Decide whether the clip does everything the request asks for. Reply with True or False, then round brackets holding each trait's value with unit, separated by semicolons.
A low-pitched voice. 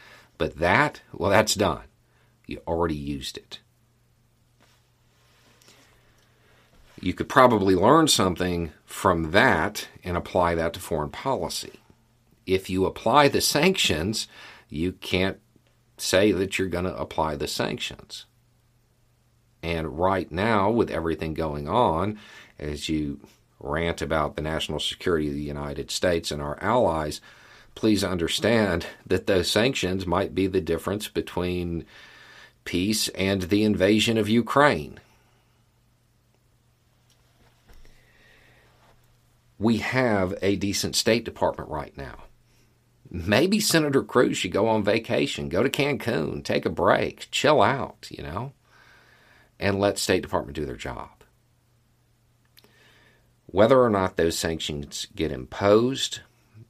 True (100 Hz)